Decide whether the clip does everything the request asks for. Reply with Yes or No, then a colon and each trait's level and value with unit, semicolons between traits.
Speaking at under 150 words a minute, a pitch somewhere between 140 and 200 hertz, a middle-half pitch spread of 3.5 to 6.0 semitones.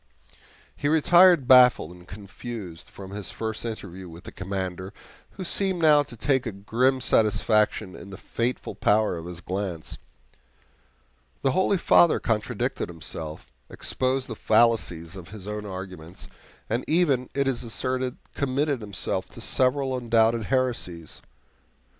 No: slow, 135 wpm; low, 115 Hz; wide, 5.4 semitones